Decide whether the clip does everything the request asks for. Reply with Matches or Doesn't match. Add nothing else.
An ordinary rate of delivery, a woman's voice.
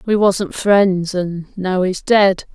Matches